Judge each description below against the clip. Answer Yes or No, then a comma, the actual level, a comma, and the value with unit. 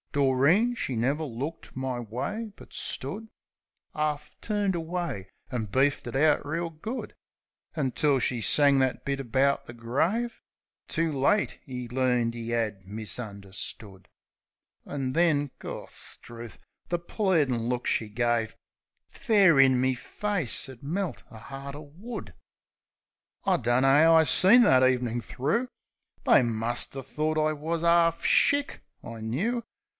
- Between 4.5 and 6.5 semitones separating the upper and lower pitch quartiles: Yes, wide, 5.5 semitones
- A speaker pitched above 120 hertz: Yes, low, 135 Hz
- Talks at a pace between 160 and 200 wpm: No, slow, 135 wpm